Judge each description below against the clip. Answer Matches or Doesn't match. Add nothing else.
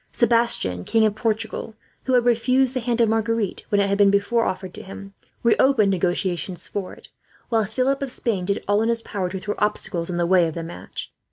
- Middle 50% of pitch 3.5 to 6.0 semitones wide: Matches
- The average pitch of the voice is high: Matches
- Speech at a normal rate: Doesn't match